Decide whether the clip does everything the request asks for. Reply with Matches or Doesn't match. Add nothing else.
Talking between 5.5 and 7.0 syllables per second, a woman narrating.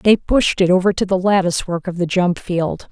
Doesn't match